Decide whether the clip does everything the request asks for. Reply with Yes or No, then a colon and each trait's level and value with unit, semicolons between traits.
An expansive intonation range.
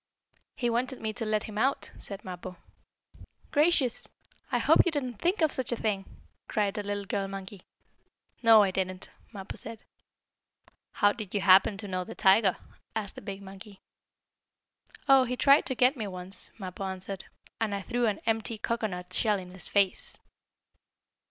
No: average, 3.3 semitones